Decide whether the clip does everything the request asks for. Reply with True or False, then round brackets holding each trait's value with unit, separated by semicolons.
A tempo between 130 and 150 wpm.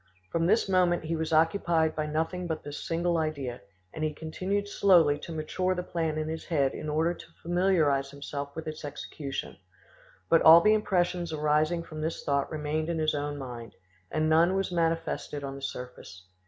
False (185 wpm)